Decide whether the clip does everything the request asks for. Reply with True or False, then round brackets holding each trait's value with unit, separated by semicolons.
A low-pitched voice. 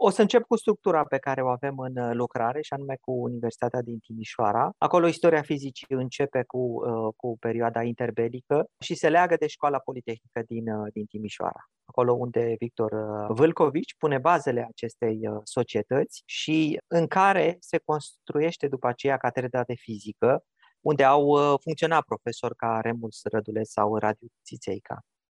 True (125 Hz)